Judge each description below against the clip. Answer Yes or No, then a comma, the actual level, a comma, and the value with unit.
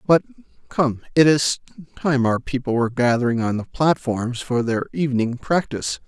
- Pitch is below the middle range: Yes, low, 130 Hz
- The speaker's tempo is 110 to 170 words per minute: Yes, average, 160 wpm